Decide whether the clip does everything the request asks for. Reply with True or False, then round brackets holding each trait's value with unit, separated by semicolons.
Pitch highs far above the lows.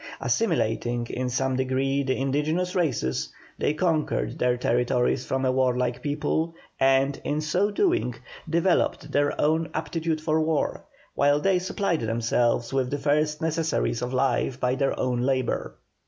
False (4.0 semitones)